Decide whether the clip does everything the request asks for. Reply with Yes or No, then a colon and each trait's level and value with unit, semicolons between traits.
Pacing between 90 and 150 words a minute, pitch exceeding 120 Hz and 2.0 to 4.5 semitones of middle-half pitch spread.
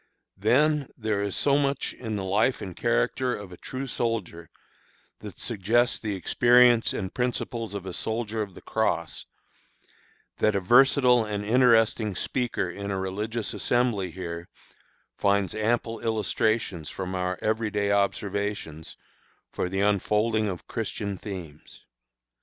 No: slow, 135 wpm; low, 105 Hz; average, 3.5 semitones